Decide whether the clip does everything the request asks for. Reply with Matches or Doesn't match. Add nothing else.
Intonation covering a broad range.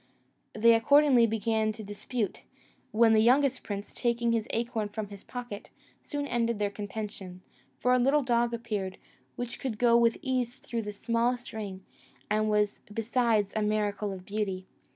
Doesn't match